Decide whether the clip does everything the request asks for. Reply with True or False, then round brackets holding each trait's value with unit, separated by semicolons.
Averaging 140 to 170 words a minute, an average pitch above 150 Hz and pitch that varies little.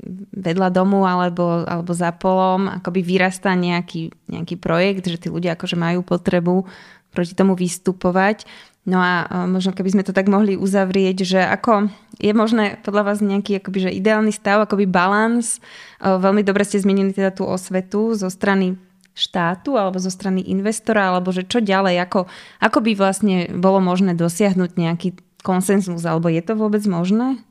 True (160 wpm; 190 Hz; 2.0 semitones)